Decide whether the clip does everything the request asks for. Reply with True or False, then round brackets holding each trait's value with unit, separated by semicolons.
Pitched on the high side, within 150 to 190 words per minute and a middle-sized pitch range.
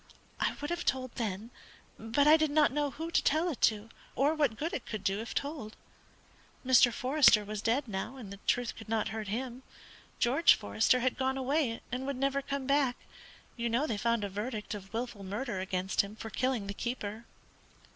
False (240 Hz; 200 wpm; 4.3 semitones)